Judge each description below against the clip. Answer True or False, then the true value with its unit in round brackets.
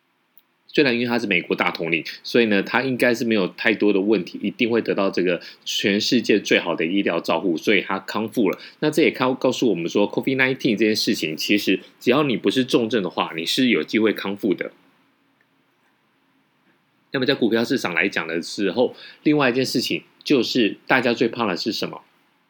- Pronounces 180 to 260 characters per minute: False (325 characters per minute)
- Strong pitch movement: False (3.0 semitones)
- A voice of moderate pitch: False (120 Hz)